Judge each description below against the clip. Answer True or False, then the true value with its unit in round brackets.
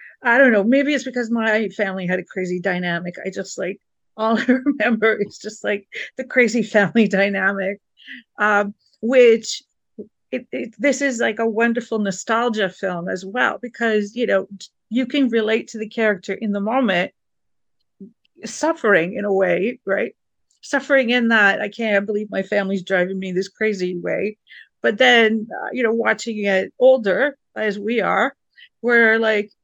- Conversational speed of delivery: True (165 wpm)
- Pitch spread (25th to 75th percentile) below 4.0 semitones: True (3.3 semitones)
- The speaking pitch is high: True (220 Hz)